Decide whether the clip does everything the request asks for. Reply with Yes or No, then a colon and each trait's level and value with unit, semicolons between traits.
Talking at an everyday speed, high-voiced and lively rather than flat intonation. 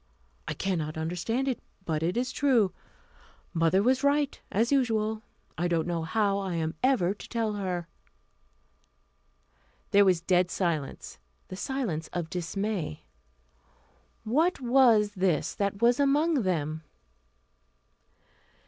No: slow, 125 wpm; high, 200 Hz; wide, 5.9 semitones